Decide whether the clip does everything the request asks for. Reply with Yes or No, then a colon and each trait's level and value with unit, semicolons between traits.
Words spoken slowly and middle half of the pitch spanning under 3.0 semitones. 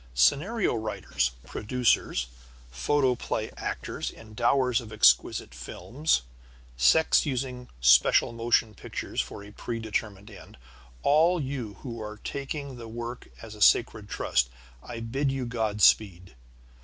No: slow, 120 wpm; average, 4.0 semitones